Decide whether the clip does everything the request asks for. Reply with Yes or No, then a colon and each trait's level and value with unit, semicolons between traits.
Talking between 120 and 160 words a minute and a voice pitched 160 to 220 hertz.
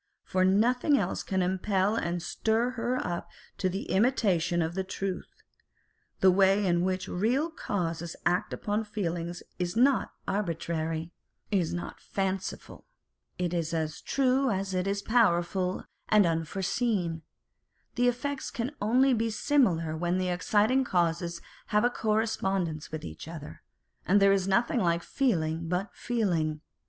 Yes: average, 145 wpm; high, 190 Hz